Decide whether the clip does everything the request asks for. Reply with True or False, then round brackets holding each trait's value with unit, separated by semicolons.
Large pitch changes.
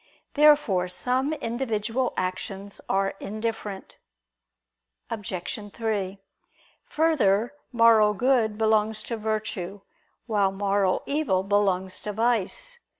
False (3.1 semitones)